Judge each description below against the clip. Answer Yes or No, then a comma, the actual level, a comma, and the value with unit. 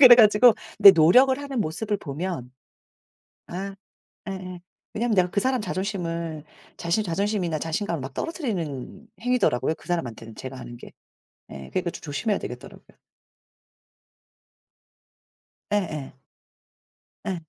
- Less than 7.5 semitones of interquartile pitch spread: Yes, average, 5.1 semitones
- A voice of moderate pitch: Yes, medium, 180 Hz